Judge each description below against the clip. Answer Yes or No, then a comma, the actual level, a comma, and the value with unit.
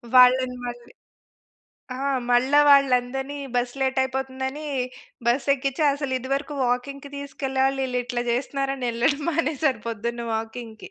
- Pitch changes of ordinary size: No, narrow, 2.1 semitones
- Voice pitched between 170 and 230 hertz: No, very high, 260 Hz